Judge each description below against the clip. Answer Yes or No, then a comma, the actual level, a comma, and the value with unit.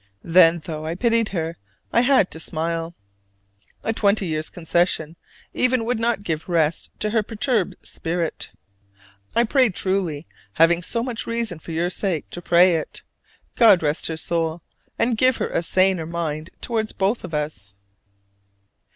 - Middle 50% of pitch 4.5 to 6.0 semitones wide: Yes, average, 5.3 semitones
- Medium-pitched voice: Yes, medium, 175 Hz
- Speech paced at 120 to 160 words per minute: Yes, average, 155 wpm